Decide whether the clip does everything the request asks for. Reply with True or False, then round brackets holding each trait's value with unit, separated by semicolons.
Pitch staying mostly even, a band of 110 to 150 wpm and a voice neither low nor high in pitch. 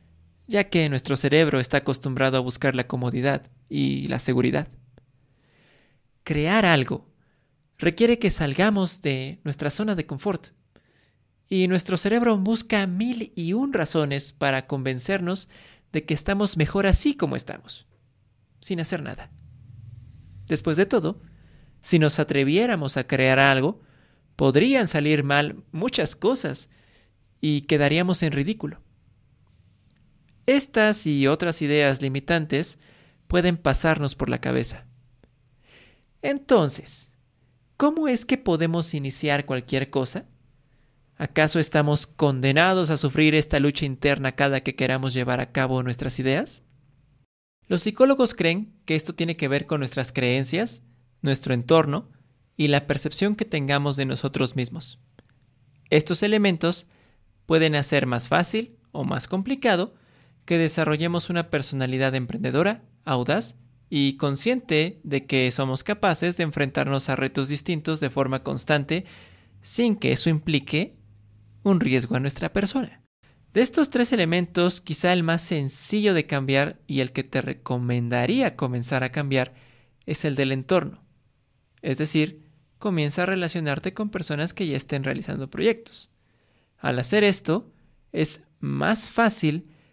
False (4.7 semitones; 130 wpm; 145 Hz)